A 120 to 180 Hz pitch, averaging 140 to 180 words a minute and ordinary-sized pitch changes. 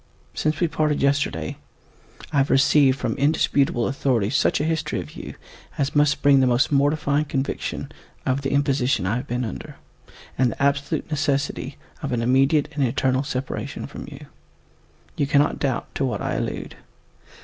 No: medium, 140 Hz; average, 165 wpm; narrow, 1.8 semitones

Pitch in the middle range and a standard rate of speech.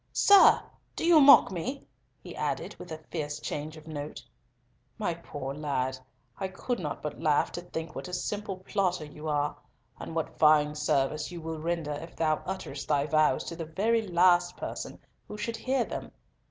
Yes: medium, 165 Hz; average, 180 wpm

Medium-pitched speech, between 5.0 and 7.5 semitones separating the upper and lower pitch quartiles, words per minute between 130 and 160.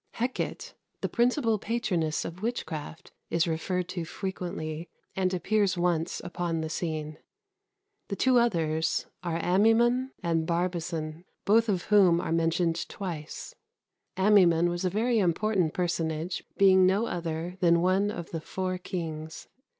No: medium, 175 Hz; average, 3.3 semitones; slow, 135 wpm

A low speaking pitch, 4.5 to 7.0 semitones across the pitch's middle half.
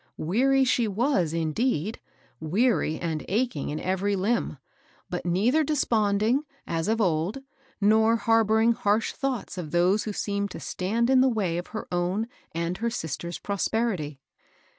No: high, 205 Hz; average, 4.9 semitones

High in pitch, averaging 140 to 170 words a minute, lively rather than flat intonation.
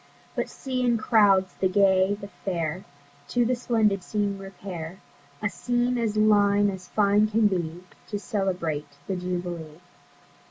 No: high, 200 Hz; average, 145 wpm; average, 2.9 semitones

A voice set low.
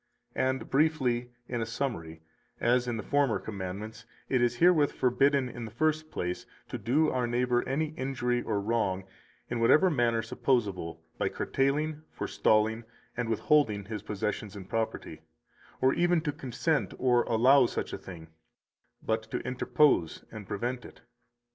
Yes: low, 120 Hz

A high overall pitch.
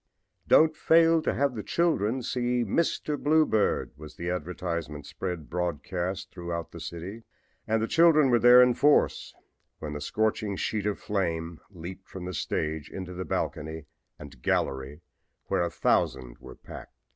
No: very low, 90 Hz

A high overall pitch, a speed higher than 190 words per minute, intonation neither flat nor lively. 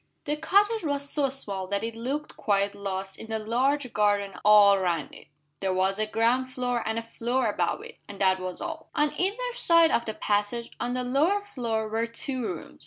No: high, 230 Hz; fast, 205 wpm; wide, 5.7 semitones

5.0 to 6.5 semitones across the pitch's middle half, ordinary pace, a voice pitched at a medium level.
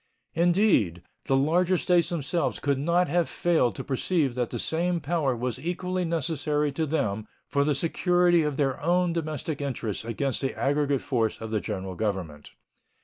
Yes: wide, 5.6 semitones; average, 165 wpm; medium, 145 Hz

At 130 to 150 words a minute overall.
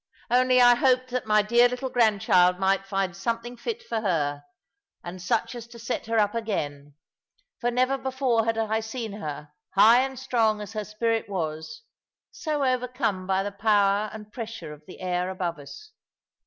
No: average, 175 wpm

